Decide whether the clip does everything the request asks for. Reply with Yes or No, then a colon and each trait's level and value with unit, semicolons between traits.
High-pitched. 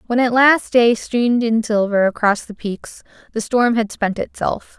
Yes: high, 225 Hz